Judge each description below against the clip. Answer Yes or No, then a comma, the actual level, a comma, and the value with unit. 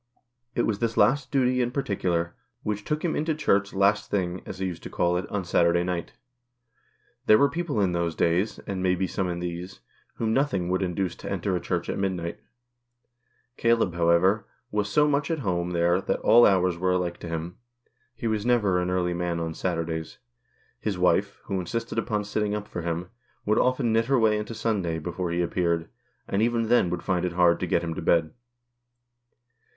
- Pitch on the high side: No, very low, 95 Hz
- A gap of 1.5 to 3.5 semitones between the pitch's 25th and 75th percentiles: No, average, 4.1 semitones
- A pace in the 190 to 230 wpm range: Yes, average, 200 wpm